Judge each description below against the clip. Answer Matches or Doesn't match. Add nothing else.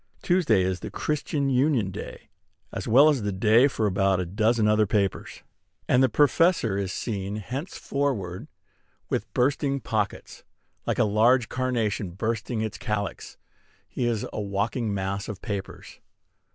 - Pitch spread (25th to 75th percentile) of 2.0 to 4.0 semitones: Doesn't match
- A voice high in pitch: Doesn't match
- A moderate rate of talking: Matches